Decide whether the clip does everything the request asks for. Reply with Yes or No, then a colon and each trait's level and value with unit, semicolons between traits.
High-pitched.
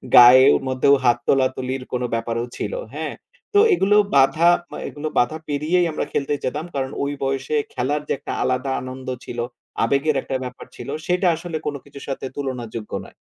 No: low, 135 Hz